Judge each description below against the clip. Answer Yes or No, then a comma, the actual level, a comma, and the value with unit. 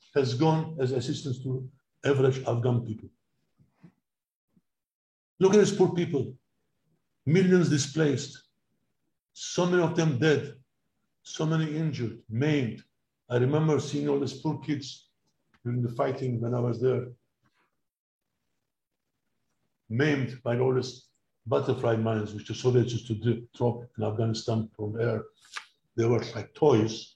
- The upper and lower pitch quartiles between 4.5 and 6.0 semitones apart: No, average, 3.7 semitones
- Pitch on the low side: Yes, low, 130 Hz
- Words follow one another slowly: Yes, slow, 130 wpm